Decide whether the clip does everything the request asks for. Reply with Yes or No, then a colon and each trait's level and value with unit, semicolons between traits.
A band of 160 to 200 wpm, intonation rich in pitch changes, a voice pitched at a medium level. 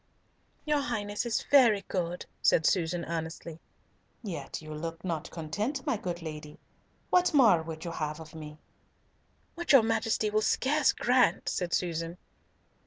No: average, 150 wpm; wide, 5.9 semitones; medium, 180 Hz